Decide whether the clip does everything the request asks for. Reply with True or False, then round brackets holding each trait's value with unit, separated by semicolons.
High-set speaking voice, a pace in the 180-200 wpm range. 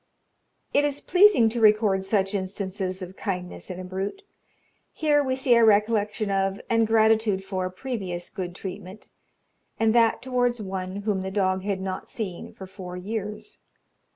False (200 Hz; 155 wpm)